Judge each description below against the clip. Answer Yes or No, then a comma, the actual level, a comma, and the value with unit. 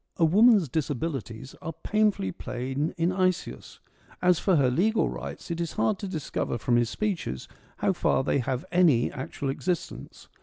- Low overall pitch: No, medium, 160 Hz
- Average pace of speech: Yes, average, 160 wpm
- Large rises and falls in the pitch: Yes, wide, 5.8 semitones